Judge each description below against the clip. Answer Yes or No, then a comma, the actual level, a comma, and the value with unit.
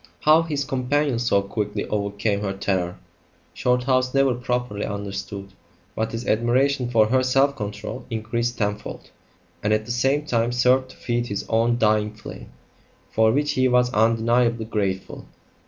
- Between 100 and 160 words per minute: Yes, average, 150 wpm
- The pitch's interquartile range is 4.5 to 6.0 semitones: No, average, 3.4 semitones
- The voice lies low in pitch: Yes, low, 115 Hz